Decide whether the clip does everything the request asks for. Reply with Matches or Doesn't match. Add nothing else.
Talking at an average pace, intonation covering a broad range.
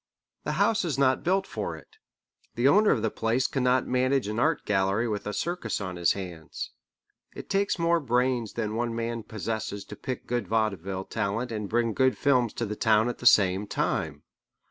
Doesn't match